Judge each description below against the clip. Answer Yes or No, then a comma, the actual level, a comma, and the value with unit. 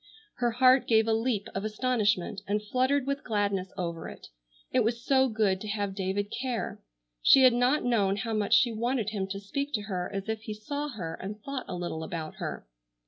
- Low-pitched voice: No, high, 215 Hz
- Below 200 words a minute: No, fast, 205 wpm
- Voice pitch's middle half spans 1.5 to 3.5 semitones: No, average, 4.1 semitones